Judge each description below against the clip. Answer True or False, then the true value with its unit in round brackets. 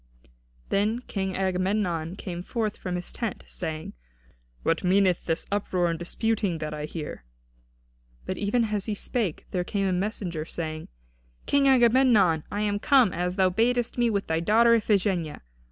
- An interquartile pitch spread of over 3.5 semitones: True (4.1 semitones)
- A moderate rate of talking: True (155 wpm)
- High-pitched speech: True (195 Hz)